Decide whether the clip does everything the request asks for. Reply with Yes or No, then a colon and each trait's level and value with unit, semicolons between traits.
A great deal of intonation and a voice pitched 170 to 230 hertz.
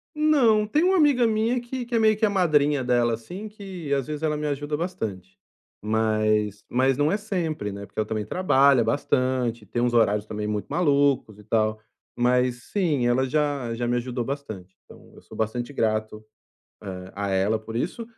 No: wide, 8.3 semitones; low, 130 Hz